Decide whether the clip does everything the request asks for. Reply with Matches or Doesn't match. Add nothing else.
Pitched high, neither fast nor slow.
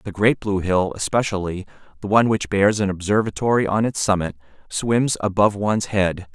Doesn't match